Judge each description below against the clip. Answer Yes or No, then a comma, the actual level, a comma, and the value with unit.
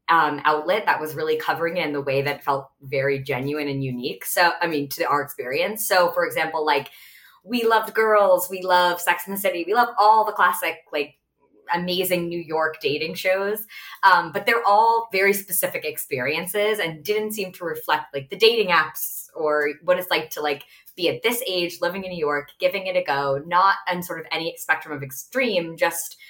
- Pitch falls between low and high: Yes, medium, 175 Hz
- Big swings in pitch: No, average, 4.8 semitones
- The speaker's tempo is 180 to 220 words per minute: Yes, fast, 205 wpm